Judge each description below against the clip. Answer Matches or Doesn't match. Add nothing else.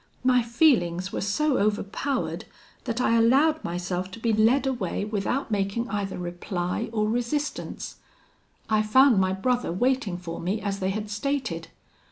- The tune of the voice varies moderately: Matches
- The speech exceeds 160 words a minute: Doesn't match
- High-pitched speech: Matches